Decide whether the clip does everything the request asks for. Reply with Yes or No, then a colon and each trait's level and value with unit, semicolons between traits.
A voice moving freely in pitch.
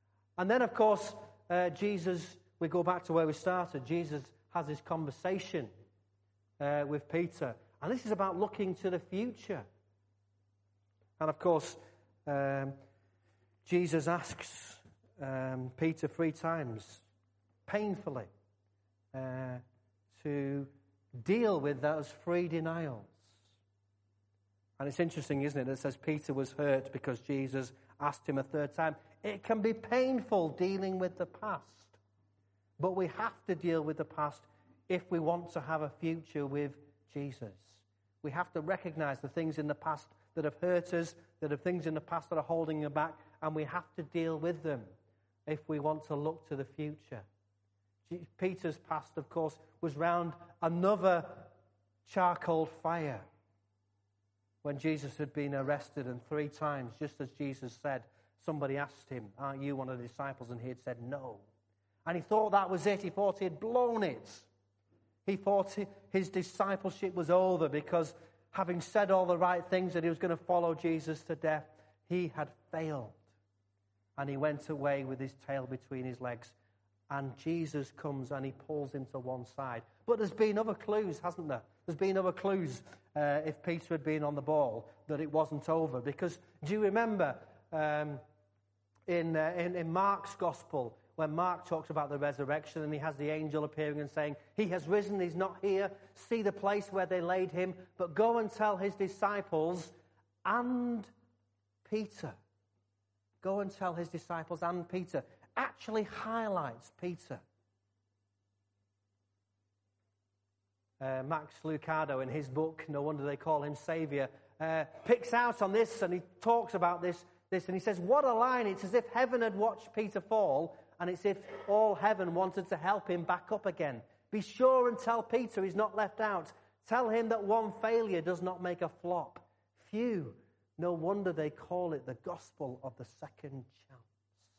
Yes: wide, 6.4 semitones